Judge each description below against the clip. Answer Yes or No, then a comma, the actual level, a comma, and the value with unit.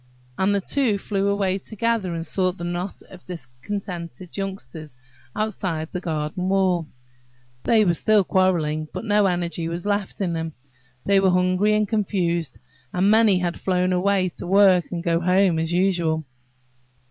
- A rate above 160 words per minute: No, average, 155 wpm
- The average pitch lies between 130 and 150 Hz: No, medium, 185 Hz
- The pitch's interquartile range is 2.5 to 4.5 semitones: Yes, average, 2.8 semitones